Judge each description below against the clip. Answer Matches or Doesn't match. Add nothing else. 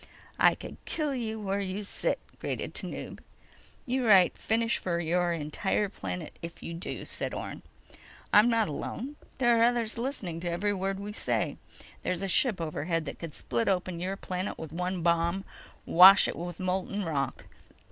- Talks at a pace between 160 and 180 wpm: Matches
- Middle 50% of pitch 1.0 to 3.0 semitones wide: Doesn't match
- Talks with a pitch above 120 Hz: Matches